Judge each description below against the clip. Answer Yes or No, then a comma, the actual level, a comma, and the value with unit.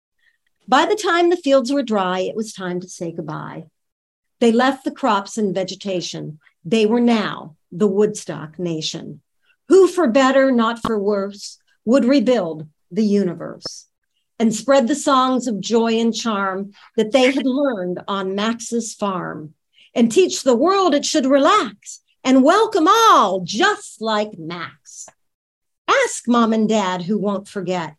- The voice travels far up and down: Yes, wide, 6.1 semitones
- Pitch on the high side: Yes, high, 225 Hz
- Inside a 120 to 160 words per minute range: Yes, average, 150 wpm